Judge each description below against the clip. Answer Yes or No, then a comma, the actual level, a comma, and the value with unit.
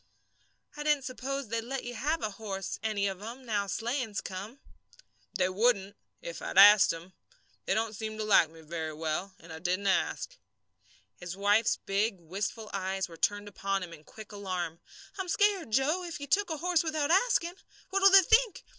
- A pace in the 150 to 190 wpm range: Yes, average, 185 wpm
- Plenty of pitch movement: Yes, wide, 6.6 semitones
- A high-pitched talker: Yes, high, 215 Hz